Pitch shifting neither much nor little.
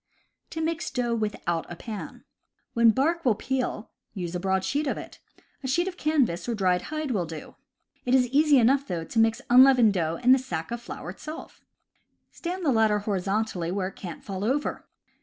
No: wide, 6.2 semitones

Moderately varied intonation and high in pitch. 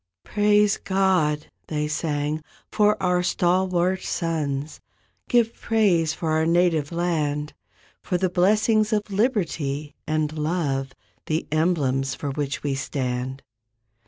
No: average, 4.1 semitones; medium, 165 Hz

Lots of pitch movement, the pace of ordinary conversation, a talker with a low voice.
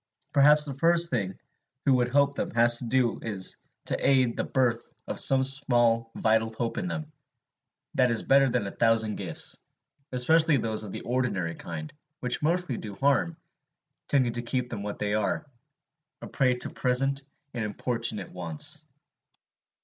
No: average, 3.6 semitones; average, 165 wpm; low, 120 Hz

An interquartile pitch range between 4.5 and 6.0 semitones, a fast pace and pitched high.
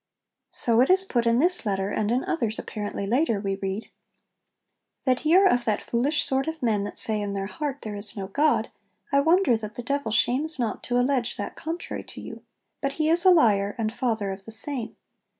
Yes: wide, 5.6 semitones; fast, 215 wpm; high, 240 Hz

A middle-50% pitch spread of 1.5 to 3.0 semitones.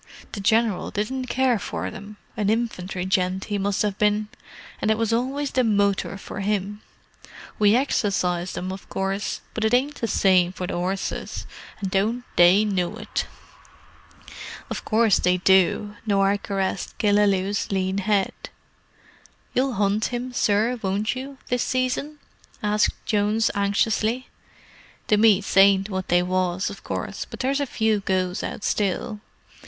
Yes: average, 2.7 semitones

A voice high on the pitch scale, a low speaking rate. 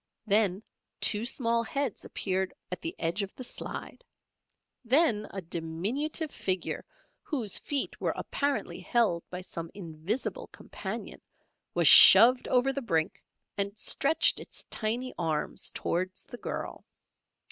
Yes: high, 215 Hz; slow, 125 wpm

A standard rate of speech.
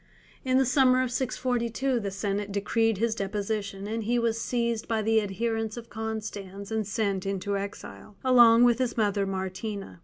Yes: average, 165 wpm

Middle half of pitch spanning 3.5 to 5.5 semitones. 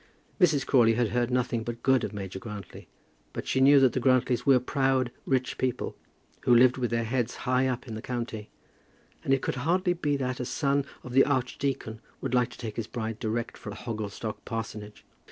No: average, 2.7 semitones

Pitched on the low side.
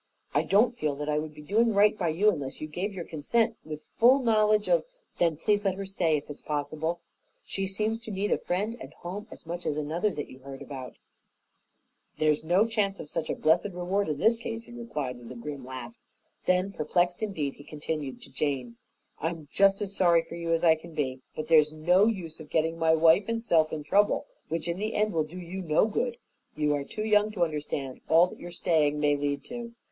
No: medium, 170 Hz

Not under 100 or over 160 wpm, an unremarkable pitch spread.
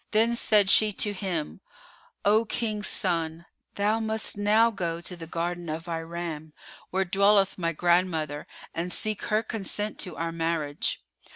Yes: average, 150 wpm; average, 4.0 semitones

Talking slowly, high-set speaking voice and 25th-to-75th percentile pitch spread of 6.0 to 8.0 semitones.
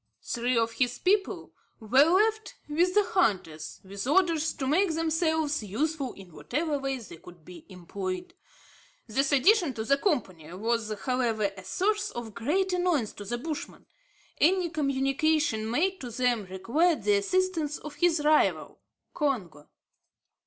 No: average, 145 wpm; very high, 275 Hz; wide, 7.0 semitones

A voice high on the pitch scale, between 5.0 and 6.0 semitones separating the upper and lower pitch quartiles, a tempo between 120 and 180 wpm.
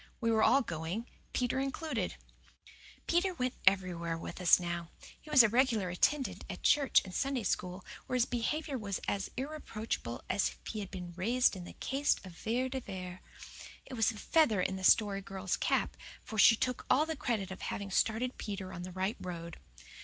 No: high, 215 Hz; wide, 5.6 semitones; average, 190 wpm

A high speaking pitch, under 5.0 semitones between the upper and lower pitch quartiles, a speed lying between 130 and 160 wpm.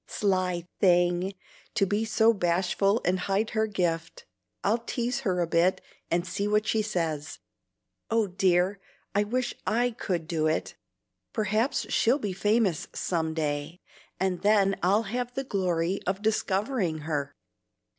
Yes: high, 195 Hz; average, 3.8 semitones; average, 145 wpm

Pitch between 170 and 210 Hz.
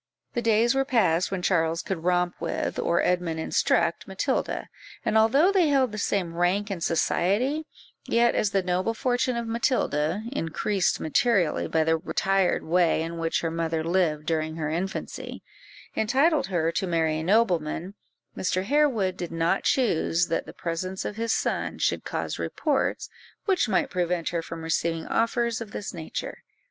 Yes: medium, 185 Hz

